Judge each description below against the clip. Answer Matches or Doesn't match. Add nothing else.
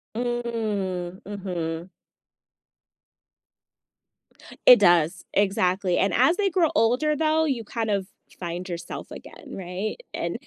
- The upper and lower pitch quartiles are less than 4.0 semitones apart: Doesn't match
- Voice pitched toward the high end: Matches